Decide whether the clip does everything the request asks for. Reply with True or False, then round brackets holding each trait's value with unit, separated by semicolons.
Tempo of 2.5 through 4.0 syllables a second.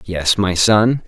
True (3.1 syllables/s)